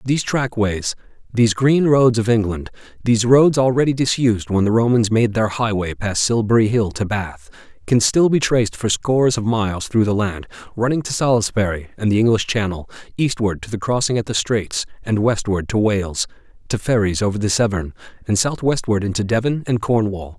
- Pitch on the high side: No, low, 110 Hz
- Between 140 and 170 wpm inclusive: No, average, 185 wpm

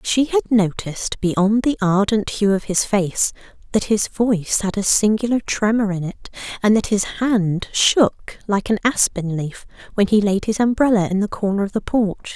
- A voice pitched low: No, high, 210 Hz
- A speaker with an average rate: Yes, average, 190 wpm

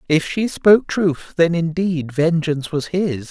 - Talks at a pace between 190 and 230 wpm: No, average, 165 wpm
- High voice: No, medium, 165 Hz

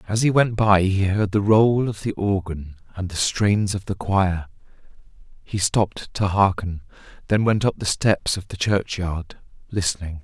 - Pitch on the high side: No, very low, 95 Hz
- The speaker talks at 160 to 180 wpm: Yes, average, 175 wpm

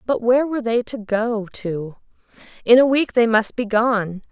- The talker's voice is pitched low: No, high, 230 Hz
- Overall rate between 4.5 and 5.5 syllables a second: Yes, 4.6 syllables/s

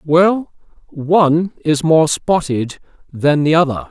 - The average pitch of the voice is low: No, medium, 155 Hz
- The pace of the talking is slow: Yes, slow, 125 wpm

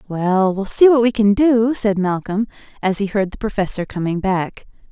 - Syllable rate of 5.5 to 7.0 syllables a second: No, 4.8 syllables/s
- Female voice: Yes, female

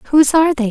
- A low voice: No, very high, 285 Hz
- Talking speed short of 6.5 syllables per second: No, 6.9 syllables/s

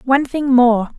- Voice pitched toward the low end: No, very high, 255 Hz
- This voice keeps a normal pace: Yes, average, 185 wpm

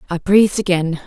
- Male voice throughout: No, female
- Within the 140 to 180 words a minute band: Yes, average, 170 wpm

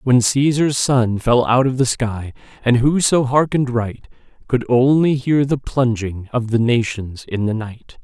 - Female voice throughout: No, male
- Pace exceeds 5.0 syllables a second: No, 4.2 syllables/s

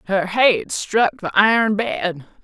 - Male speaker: No, female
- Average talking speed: Yes, average, 150 wpm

